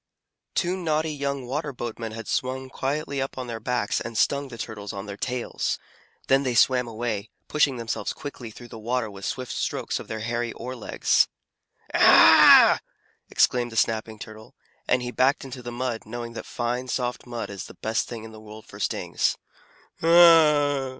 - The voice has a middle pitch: No, low, 120 Hz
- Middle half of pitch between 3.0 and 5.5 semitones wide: No, narrow, 2.6 semitones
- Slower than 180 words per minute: No, average, 185 wpm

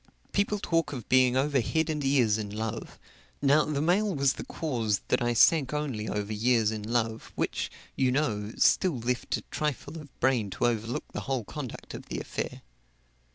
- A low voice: Yes, low, 130 Hz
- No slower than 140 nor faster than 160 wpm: No, average, 185 wpm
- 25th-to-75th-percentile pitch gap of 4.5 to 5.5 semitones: Yes, average, 5.0 semitones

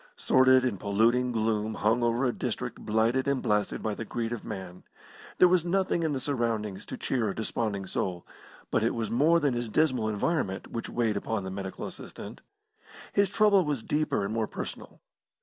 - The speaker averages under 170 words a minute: No, average, 185 wpm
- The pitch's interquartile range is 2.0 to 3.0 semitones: No, average, 4.4 semitones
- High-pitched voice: No, low, 115 Hz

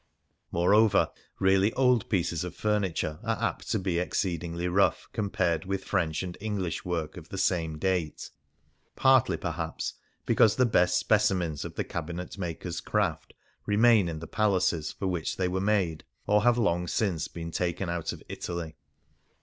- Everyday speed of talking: Yes, average, 160 wpm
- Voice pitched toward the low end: Yes, very low, 90 Hz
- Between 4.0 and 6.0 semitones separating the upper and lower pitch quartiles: No, average, 3.4 semitones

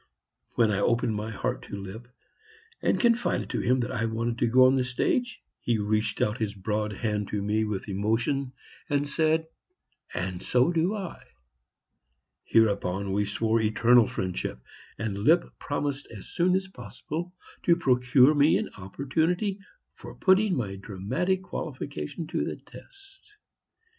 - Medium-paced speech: Yes, average, 150 wpm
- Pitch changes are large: Yes, wide, 7.2 semitones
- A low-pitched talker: Yes, low, 120 Hz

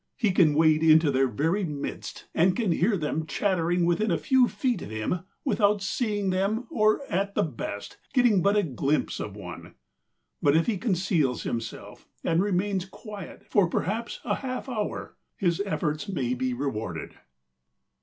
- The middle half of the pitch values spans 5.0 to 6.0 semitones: Yes, wide, 5.6 semitones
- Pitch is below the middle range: No, medium, 180 Hz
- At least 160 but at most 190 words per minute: Yes, average, 165 wpm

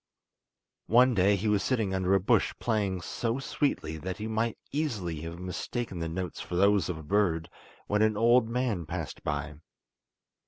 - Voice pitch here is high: No, low, 100 Hz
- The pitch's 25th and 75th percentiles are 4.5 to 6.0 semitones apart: Yes, average, 4.8 semitones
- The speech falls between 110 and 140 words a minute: No, average, 170 wpm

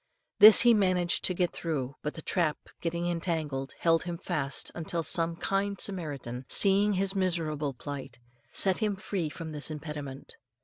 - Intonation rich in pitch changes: No, average, 3.9 semitones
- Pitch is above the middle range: No, medium, 165 Hz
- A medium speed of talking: Yes, average, 160 wpm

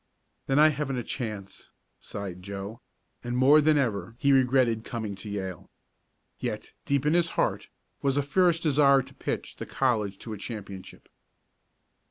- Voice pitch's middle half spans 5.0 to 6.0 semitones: Yes, wide, 5.5 semitones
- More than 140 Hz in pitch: No, low, 125 Hz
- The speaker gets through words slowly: No, average, 160 wpm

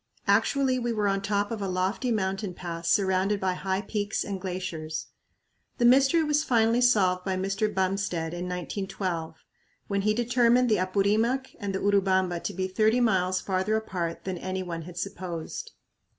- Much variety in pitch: No, average, 3.1 semitones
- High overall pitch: Yes, high, 195 Hz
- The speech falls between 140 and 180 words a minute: Yes, average, 165 wpm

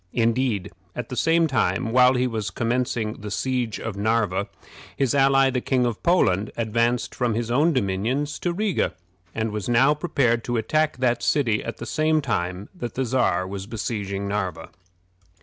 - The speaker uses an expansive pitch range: No, average, 3.9 semitones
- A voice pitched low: Yes, low, 120 Hz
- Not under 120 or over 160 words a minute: No, average, 170 wpm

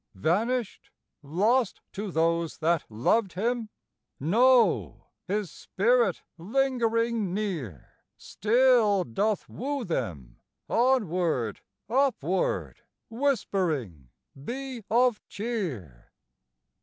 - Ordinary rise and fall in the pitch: No, wide, 6.9 semitones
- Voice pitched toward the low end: No, high, 210 Hz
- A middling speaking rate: No, slow, 80 wpm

